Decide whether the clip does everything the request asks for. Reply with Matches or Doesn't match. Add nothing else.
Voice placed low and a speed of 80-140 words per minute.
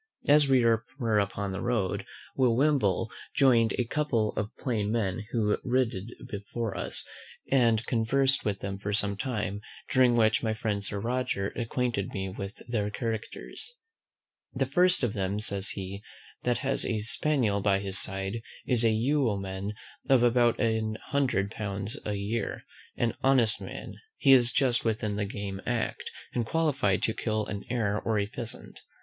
Doesn't match